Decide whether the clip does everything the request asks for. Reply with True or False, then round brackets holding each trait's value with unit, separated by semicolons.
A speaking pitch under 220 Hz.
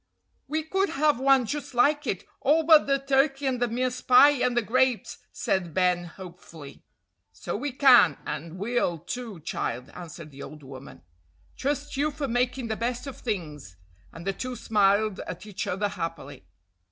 False (235 Hz)